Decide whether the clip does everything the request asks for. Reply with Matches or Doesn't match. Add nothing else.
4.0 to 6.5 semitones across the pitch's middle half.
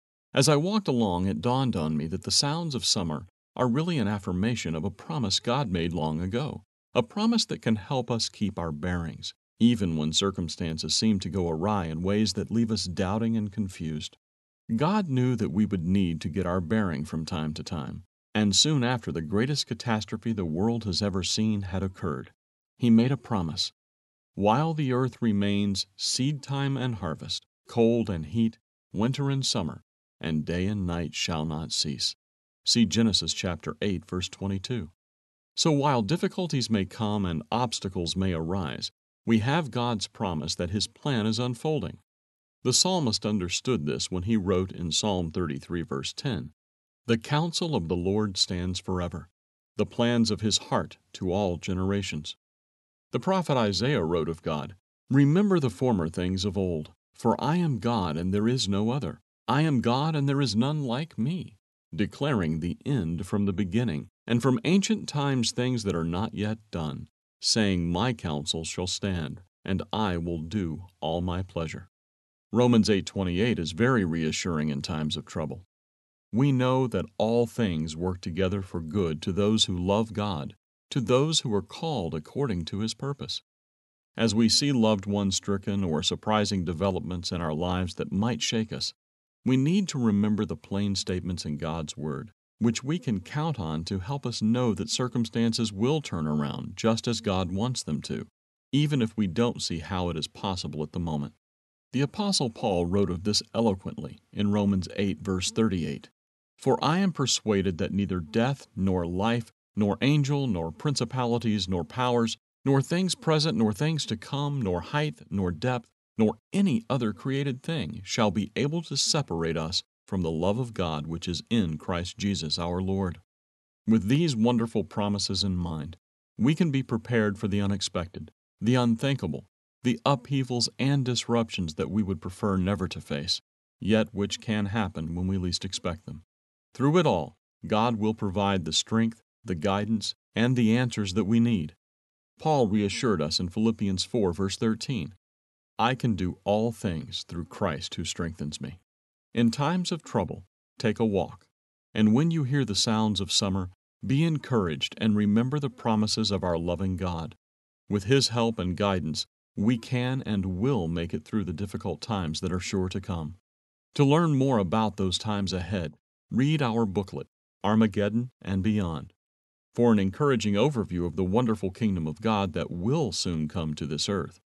Matches